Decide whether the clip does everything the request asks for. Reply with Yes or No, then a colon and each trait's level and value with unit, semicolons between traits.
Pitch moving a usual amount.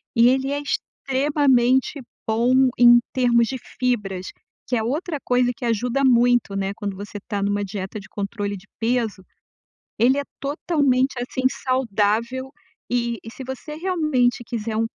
Yes: average, 3.4 semitones